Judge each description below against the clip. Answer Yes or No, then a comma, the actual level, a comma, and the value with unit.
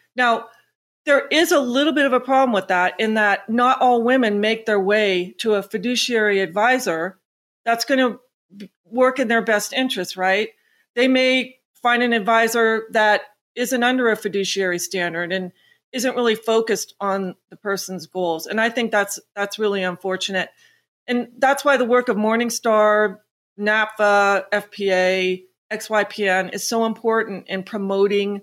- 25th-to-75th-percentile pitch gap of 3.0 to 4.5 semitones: Yes, average, 3.9 semitones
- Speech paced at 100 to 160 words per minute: Yes, average, 155 wpm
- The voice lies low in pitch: No, high, 215 Hz